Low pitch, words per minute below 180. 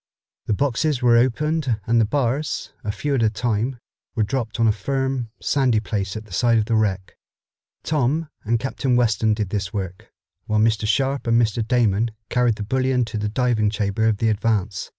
No: low, 115 Hz; average, 190 wpm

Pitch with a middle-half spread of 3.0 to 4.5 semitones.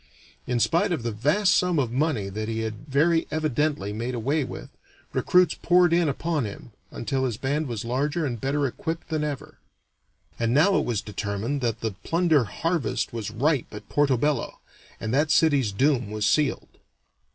No: wide, 5.4 semitones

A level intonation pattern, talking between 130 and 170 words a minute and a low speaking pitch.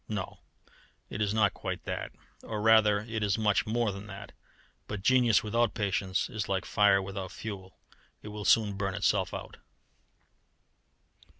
Yes: narrow, 1.9 semitones; average, 155 wpm; low, 105 Hz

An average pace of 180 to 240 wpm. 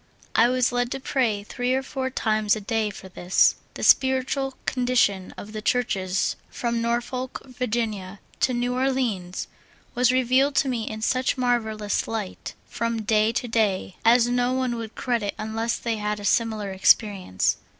No: average, 160 wpm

